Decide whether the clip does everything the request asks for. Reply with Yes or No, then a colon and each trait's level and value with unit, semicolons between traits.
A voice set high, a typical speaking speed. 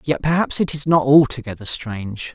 No: low, 135 Hz; average, 180 wpm